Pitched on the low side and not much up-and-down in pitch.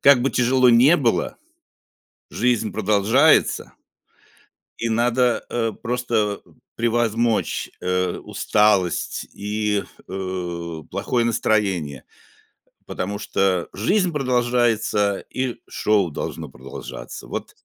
No: low, 110 Hz; average, 3.8 semitones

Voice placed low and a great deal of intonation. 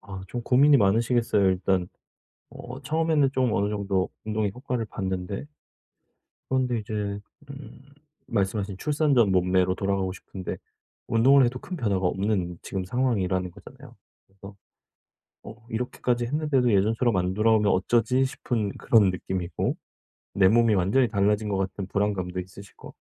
No: low, 105 Hz; average, 4.3 semitones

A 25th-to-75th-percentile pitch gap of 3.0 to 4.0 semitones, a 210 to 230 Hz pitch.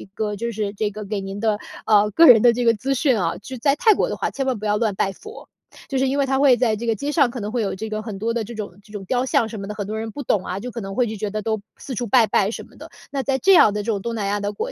Yes: average, 3.4 semitones; high, 220 Hz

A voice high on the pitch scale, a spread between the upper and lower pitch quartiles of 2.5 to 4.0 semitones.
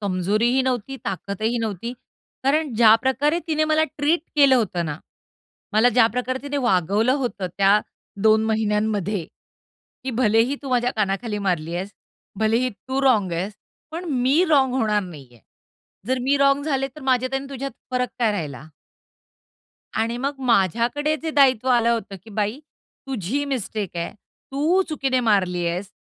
No: high, 235 Hz; average, 4.9 semitones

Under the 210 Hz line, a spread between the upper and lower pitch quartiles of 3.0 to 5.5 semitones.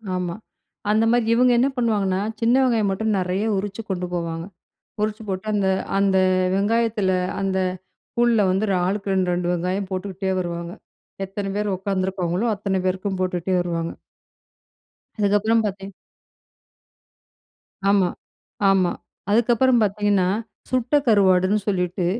No: high, 195 Hz; narrow, 2.5 semitones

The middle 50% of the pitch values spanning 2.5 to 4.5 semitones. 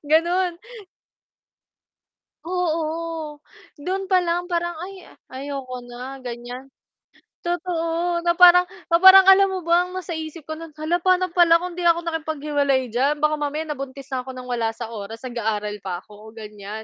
No: wide, 5.5 semitones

